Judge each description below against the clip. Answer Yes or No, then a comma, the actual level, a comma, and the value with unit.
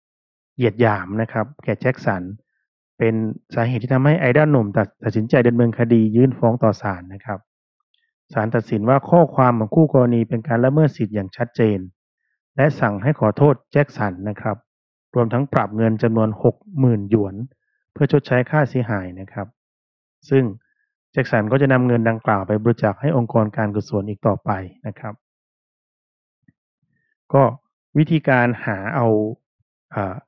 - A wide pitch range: No, average, 3.9 semitones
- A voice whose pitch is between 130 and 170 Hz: No, low, 115 Hz